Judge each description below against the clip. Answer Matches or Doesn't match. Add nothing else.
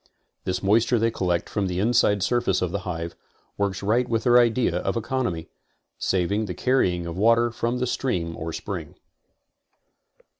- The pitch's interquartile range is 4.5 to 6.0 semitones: Matches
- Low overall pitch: Matches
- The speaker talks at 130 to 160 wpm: Doesn't match